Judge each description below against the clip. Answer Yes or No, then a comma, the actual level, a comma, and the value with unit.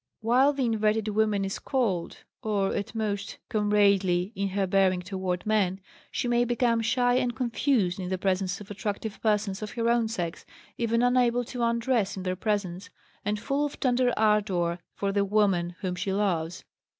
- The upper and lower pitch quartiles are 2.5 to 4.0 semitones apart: Yes, average, 3.5 semitones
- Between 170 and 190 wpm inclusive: Yes, average, 175 wpm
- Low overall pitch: No, high, 210 Hz